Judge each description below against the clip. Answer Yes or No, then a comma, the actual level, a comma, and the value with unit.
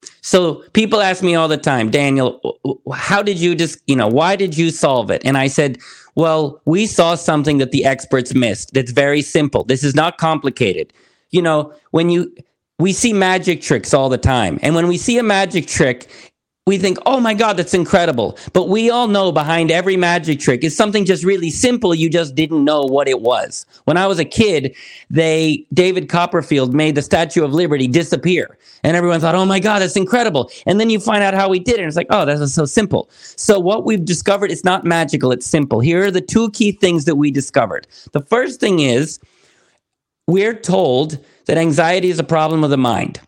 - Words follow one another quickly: Yes, fast, 210 wpm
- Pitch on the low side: No, medium, 165 Hz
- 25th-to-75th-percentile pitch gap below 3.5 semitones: No, average, 4.3 semitones